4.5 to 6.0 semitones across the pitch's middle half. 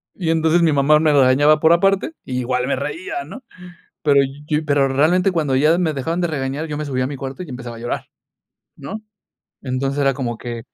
No: average, 3.6 semitones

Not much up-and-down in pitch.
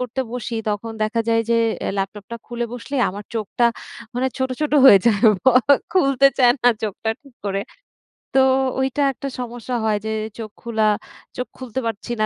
No: average, 3.0 semitones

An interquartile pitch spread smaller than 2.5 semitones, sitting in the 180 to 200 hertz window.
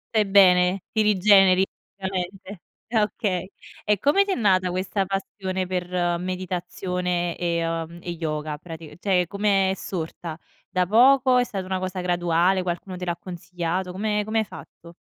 Yes: narrow, 2.1 semitones; medium, 185 Hz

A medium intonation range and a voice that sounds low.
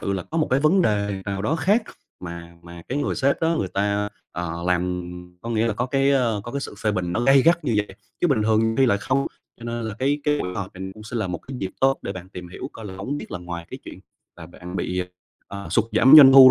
No: wide, 6.4 semitones; low, 110 Hz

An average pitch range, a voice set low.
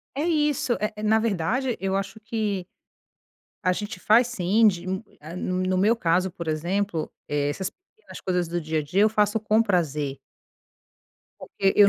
No: average, 3.9 semitones; high, 195 Hz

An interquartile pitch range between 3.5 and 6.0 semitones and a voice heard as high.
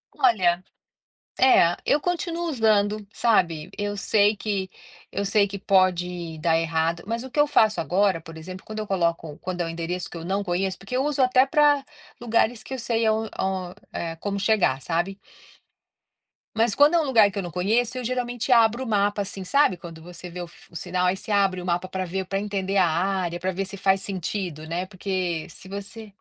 Yes: average, 3.8 semitones; high, 195 Hz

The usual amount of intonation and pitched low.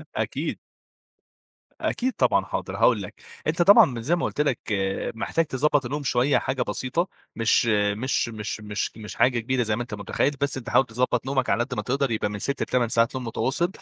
Yes: average, 3.4 semitones; low, 125 Hz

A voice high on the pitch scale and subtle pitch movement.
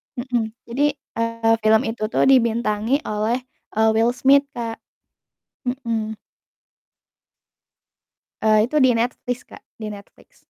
Yes: high, 230 Hz; narrow, 2.3 semitones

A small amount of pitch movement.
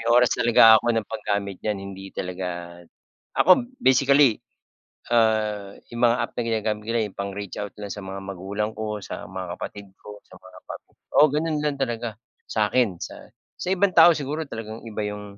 No: average, 3.4 semitones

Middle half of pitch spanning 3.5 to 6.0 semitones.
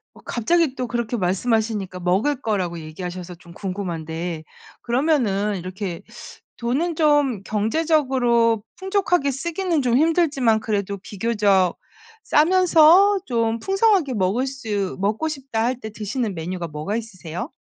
No: wide, 7.1 semitones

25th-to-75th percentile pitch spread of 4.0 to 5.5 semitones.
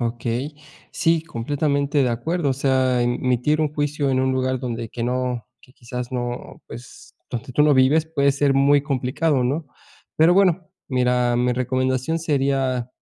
No: average, 2.8 semitones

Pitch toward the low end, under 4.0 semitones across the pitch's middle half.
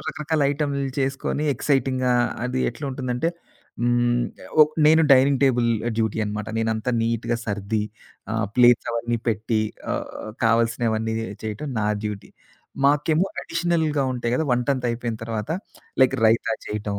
Yes: low, 120 Hz; average, 3.6 semitones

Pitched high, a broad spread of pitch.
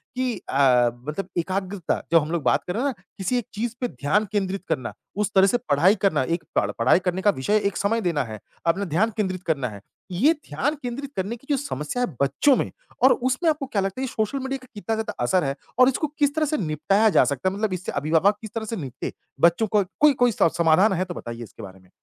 Yes: high, 195 Hz; wide, 6.6 semitones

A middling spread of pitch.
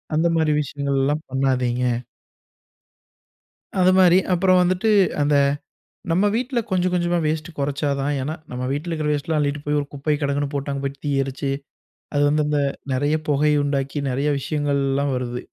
No: narrow, 2.3 semitones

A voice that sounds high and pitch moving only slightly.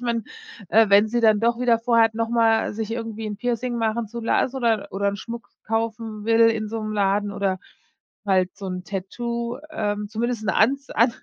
Yes: high, 225 Hz; narrow, 2.2 semitones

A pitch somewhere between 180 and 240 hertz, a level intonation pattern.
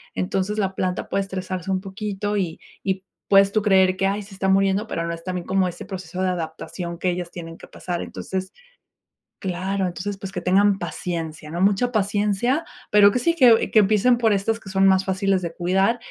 Yes: high, 190 Hz; narrow, 2.0 semitones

